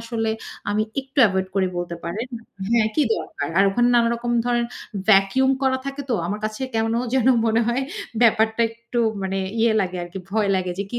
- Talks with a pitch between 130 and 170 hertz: No, high, 225 Hz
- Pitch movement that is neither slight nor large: Yes, average, 3.5 semitones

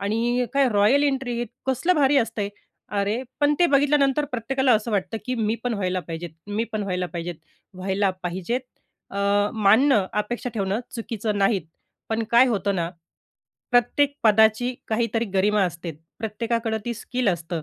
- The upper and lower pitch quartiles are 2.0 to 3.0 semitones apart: No, average, 3.9 semitones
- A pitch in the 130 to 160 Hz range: No, high, 220 Hz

